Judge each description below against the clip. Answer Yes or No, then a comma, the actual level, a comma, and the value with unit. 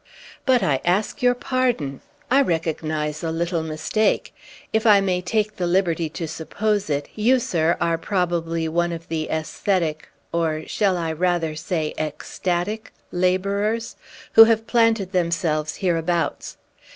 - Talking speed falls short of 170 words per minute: Yes, average, 140 wpm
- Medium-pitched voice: Yes, medium, 175 Hz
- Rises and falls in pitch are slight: No, average, 4.4 semitones